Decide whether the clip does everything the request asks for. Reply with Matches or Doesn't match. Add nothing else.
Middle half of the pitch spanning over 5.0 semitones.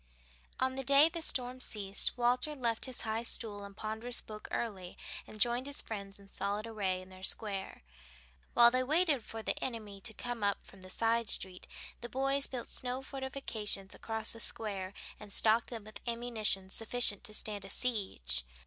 Doesn't match